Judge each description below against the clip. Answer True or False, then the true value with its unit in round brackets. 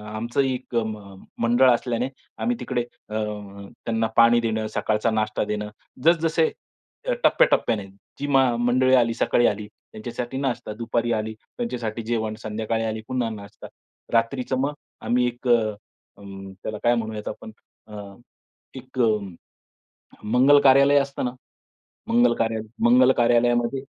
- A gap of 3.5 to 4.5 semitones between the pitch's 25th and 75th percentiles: False (2.9 semitones)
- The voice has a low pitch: True (120 Hz)